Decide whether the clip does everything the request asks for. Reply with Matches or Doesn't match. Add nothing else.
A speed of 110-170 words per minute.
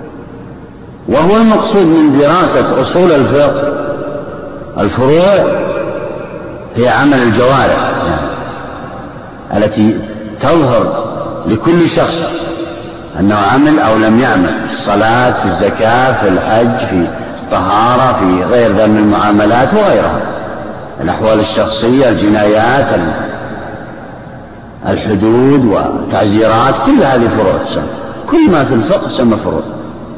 Doesn't match